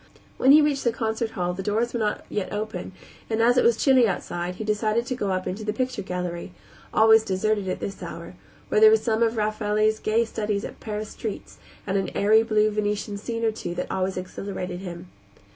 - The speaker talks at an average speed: No, fast, 210 wpm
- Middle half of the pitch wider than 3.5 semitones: No, average, 2.8 semitones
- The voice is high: Yes, high, 215 Hz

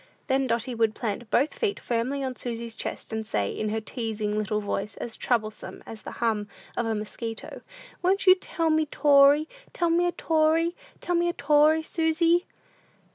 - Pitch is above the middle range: Yes, very high, 260 Hz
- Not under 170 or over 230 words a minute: Yes, average, 180 wpm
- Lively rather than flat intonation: Yes, wide, 6.4 semitones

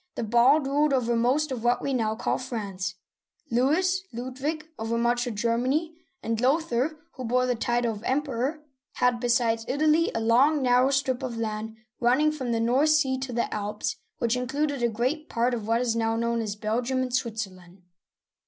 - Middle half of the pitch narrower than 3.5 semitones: Yes, average, 2.9 semitones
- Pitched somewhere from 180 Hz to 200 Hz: No, high, 245 Hz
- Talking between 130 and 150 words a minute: No, average, 190 wpm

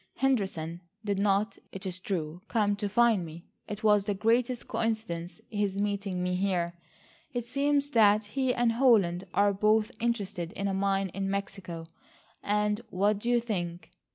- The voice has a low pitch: No, high, 205 Hz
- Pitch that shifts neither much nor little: Yes, average, 3.0 semitones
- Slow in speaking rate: No, average, 160 wpm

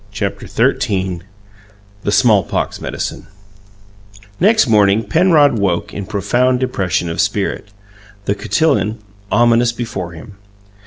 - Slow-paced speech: Yes, slow, 105 wpm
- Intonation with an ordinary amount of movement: Yes, average, 4.2 semitones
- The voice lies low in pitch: Yes, low, 105 Hz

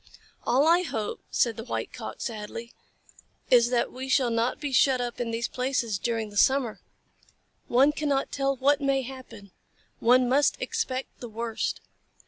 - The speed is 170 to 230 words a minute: No, average, 160 wpm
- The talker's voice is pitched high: Yes, very high, 250 Hz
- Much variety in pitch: No, average, 2.7 semitones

